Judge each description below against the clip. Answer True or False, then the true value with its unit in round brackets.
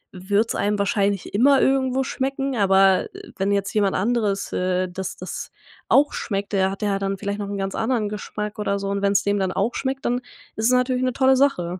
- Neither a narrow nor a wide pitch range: True (4.2 semitones)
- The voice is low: False (205 Hz)